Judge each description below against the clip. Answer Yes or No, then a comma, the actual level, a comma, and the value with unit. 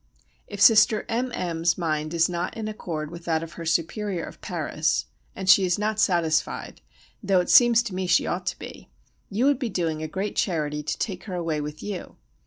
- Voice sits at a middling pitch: Yes, medium, 180 Hz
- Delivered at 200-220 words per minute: Yes, fast, 205 wpm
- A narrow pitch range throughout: No, average, 4.3 semitones